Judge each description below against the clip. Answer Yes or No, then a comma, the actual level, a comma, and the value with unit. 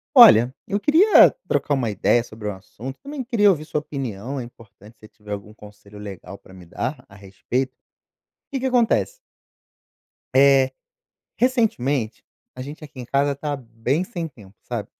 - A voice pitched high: No, low, 130 Hz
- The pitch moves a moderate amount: No, wide, 6.9 semitones